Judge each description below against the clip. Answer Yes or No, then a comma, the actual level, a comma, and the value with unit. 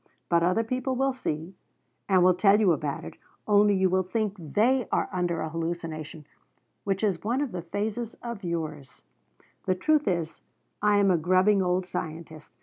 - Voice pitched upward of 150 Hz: Yes, medium, 185 Hz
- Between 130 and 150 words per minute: No, average, 175 wpm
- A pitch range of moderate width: Yes, average, 3.9 semitones